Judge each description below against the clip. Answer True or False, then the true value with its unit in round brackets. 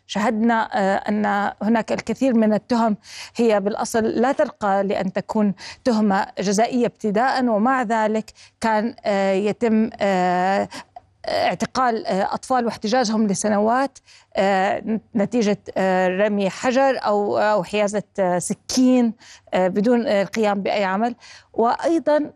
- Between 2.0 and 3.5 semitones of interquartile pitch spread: True (3.0 semitones)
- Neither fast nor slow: True (90 wpm)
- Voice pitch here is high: True (215 Hz)